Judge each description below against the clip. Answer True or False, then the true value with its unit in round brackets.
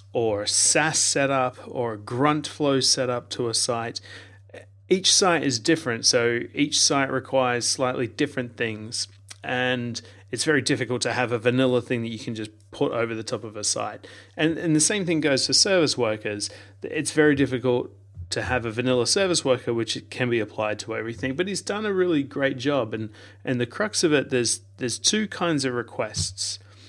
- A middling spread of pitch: True (4.1 semitones)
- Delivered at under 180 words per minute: False (190 wpm)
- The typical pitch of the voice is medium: False (125 Hz)